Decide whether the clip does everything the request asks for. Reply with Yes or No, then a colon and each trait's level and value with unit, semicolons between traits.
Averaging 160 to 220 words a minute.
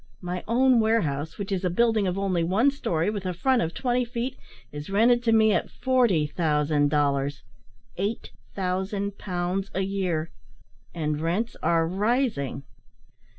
No: average, 145 wpm